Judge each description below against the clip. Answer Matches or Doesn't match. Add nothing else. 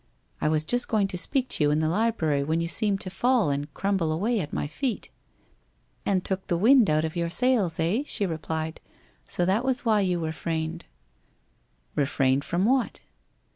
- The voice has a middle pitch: Matches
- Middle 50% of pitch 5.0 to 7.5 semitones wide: Matches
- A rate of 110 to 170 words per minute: Doesn't match